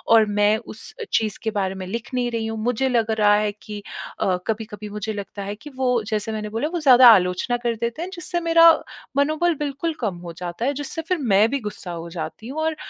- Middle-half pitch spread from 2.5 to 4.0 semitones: No, average, 4.4 semitones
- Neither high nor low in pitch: No, high, 220 Hz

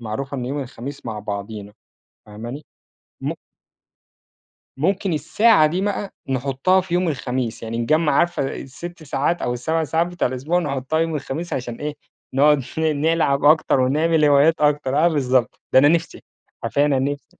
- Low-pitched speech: No, medium, 145 Hz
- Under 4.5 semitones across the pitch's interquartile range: Yes, average, 4.0 semitones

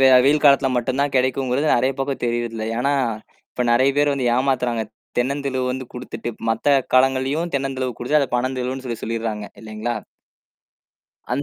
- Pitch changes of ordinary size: No, narrow, 2.3 semitones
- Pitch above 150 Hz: No, low, 130 Hz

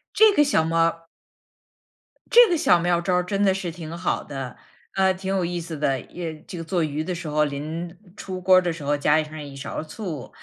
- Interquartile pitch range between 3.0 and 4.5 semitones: Yes, average, 3.3 semitones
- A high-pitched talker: No, medium, 170 Hz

